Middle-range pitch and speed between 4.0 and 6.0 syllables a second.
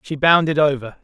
Yes: medium, 145 Hz; 5.5 syllables/s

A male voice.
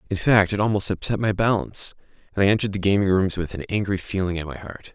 Yes: male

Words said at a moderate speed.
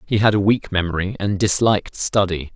Yes: average, 190 wpm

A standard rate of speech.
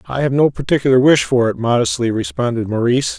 Yes: average, 190 wpm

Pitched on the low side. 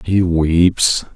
Yes: very low, 85 Hz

